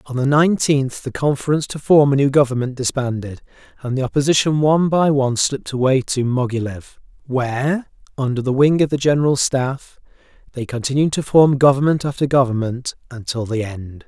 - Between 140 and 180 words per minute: Yes, average, 165 wpm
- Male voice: Yes, male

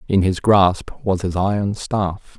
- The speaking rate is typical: Yes, average, 175 wpm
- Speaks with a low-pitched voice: Yes, very low, 95 Hz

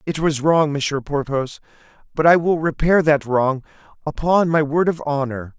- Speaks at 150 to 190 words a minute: Yes, average, 170 wpm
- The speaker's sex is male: Yes, male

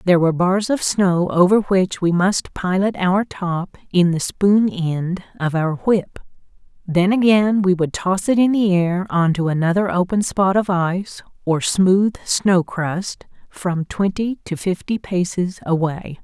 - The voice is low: No, medium, 185 Hz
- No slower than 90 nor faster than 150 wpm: No, average, 165 wpm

